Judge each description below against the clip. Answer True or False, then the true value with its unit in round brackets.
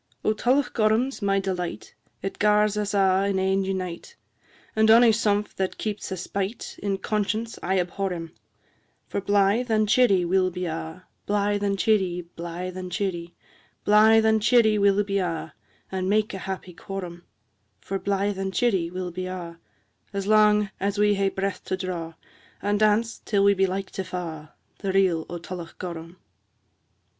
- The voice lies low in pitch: False (195 Hz)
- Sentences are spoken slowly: False (170 wpm)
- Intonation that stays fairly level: True (2.3 semitones)